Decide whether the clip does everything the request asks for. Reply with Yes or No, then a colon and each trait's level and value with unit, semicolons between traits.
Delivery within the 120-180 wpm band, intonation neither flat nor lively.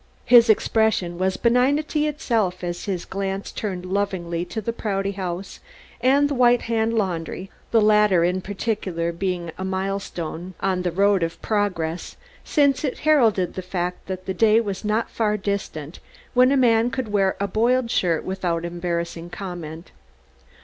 Yes: average, 155 wpm; average, 4.1 semitones